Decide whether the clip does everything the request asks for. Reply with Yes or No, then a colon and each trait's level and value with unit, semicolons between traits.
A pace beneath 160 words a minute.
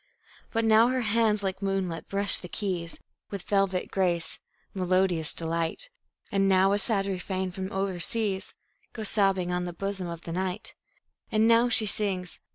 No: average, 165 wpm